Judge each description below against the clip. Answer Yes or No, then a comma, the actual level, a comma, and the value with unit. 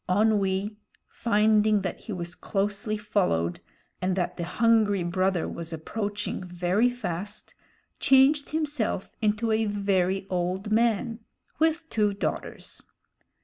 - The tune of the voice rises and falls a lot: No, average, 3.1 semitones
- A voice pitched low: No, high, 205 Hz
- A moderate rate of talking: No, slow, 115 wpm